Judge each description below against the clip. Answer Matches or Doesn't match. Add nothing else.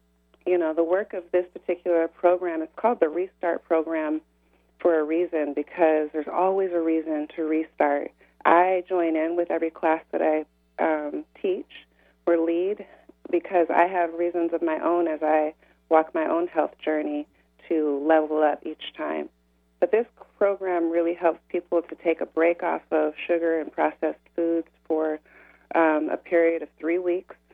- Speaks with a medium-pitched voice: Matches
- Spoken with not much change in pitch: Matches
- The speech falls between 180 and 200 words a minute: Doesn't match